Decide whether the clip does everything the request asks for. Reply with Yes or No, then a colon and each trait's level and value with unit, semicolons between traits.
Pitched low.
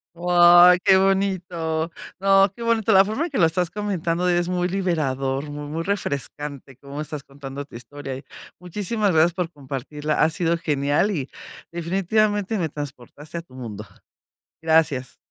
No: medium, 165 Hz